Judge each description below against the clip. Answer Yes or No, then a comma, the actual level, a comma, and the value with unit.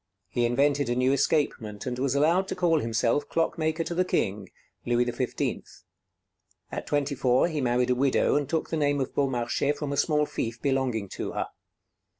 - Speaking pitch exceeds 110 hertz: Yes, low, 135 Hz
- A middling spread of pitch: Yes, average, 3.4 semitones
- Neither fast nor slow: Yes, average, 180 wpm